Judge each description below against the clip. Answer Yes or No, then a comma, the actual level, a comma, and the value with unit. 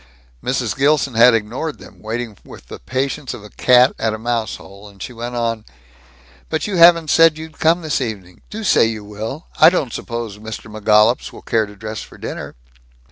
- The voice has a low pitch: Yes, low, 115 Hz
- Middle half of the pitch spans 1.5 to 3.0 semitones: No, wide, 5.4 semitones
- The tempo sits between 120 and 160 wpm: No, average, 195 wpm